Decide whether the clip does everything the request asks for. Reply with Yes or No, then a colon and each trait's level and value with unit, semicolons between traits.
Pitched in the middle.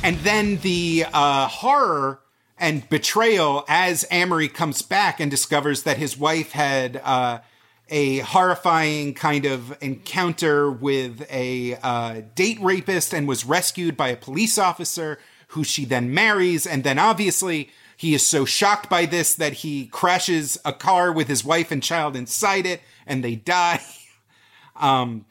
Yes: medium, 150 Hz